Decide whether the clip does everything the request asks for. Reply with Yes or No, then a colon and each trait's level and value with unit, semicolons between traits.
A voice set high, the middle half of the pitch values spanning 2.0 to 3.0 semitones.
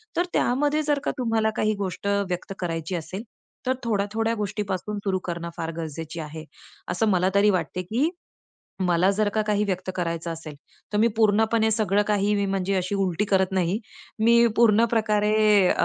No: high, 200 Hz; average, 3.5 semitones